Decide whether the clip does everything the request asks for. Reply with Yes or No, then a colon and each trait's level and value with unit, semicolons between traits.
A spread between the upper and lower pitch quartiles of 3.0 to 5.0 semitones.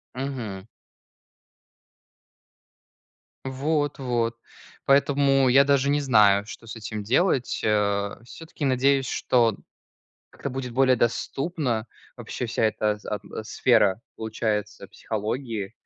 Yes: average, 4.1 semitones